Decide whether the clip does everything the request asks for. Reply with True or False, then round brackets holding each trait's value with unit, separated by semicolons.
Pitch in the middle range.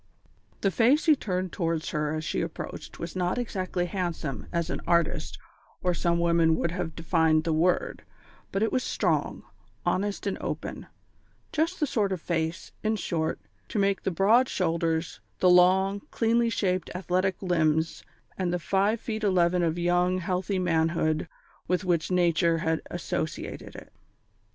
True (180 Hz)